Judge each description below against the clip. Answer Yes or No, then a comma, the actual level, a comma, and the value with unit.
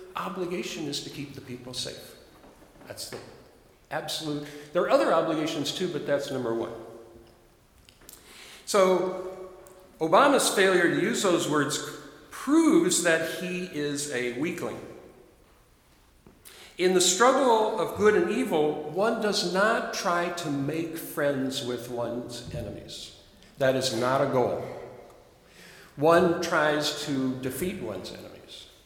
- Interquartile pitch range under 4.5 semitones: No, average, 4.8 semitones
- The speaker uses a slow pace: Yes, slow, 125 wpm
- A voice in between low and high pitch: Yes, medium, 155 Hz